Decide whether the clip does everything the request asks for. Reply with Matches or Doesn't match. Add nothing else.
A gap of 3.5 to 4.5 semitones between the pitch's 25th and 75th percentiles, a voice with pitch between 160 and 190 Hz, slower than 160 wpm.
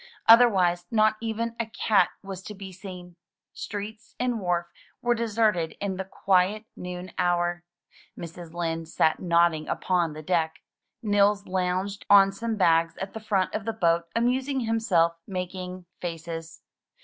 Matches